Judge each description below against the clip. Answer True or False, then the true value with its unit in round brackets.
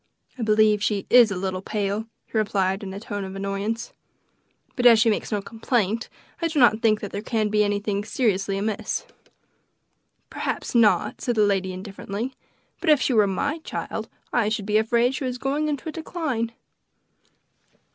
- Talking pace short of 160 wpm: False (175 wpm)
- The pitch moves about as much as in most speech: True (3.2 semitones)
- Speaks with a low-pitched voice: False (215 Hz)